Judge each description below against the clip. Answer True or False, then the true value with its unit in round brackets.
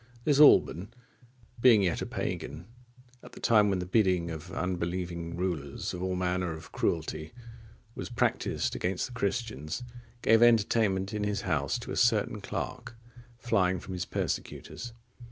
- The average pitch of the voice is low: True (95 Hz)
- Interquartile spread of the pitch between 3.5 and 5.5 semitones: True (4.6 semitones)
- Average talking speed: True (150 wpm)